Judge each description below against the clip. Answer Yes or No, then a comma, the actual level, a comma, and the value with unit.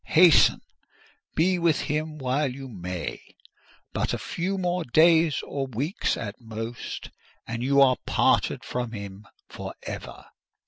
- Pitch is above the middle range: No, low, 135 Hz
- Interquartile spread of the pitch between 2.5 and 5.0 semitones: No, wide, 5.6 semitones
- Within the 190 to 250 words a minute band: No, slow, 135 wpm